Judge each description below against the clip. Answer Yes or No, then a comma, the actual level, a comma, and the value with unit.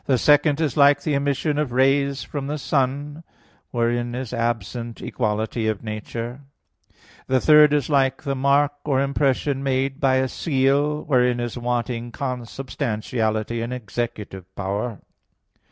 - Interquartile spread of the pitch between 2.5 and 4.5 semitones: Yes, average, 3.1 semitones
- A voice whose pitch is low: Yes, low, 130 Hz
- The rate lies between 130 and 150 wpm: Yes, slow, 135 wpm